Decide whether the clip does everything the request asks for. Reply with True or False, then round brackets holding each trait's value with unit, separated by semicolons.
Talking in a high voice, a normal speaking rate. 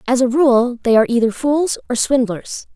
True (250 Hz; 195 wpm)